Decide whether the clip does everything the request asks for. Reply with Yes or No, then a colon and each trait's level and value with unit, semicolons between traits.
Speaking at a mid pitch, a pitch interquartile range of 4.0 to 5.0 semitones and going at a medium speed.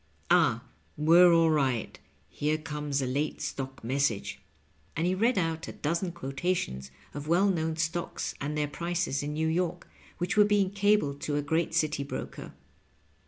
No: medium, 160 Hz; average, 3.3 semitones; average, 165 wpm